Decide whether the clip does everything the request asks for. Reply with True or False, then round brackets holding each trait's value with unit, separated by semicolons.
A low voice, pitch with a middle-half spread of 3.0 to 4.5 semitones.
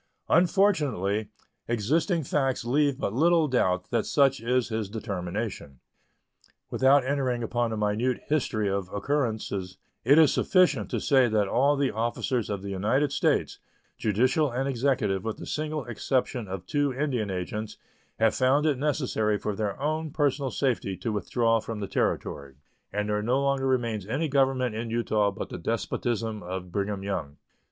False (120 Hz; 5.0 semitones)